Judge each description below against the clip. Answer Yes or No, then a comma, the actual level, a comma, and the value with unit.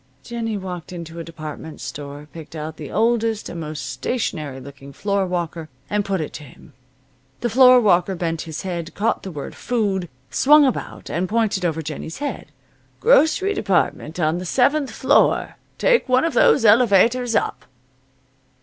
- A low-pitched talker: No, medium, 185 Hz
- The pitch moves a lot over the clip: Yes, wide, 6.6 semitones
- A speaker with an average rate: Yes, average, 155 wpm